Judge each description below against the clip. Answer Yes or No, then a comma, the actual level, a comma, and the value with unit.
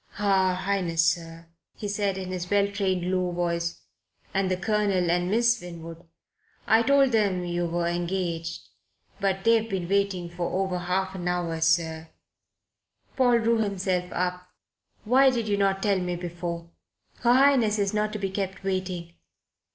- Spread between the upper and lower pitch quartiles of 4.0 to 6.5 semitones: No, average, 2.7 semitones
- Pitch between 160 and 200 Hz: Yes, medium, 185 Hz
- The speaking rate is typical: Yes, average, 160 wpm